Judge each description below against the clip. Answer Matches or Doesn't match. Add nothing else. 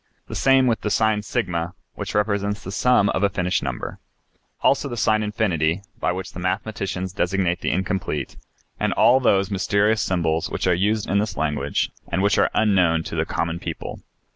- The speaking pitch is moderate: Doesn't match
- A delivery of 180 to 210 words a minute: Matches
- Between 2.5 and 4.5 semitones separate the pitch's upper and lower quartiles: Matches